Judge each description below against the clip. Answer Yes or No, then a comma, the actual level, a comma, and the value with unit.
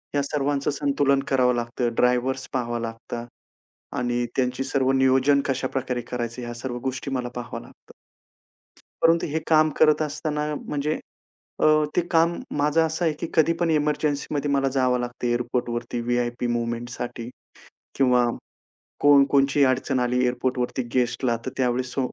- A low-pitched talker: Yes, low, 130 Hz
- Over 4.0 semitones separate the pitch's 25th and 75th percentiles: No, average, 2.8 semitones